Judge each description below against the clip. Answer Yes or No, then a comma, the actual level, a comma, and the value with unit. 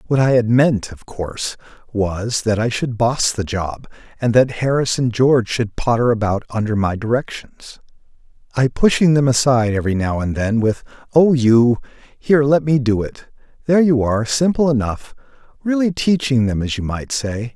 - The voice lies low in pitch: Yes, low, 120 Hz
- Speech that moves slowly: No, average, 175 wpm